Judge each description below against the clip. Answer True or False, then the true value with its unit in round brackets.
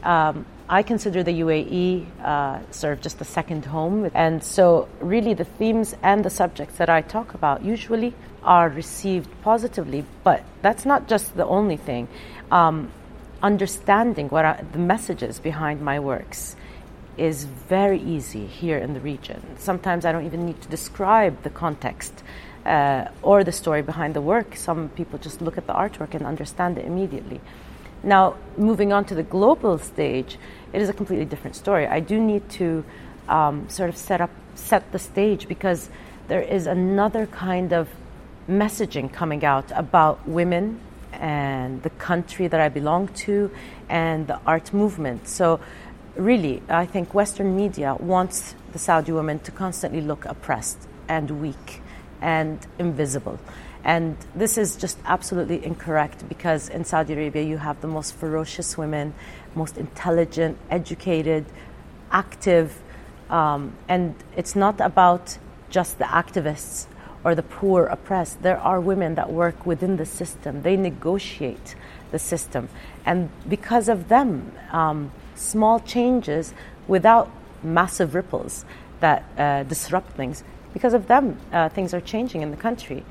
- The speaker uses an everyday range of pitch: True (3.9 semitones)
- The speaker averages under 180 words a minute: True (150 wpm)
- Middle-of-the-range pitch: True (170 Hz)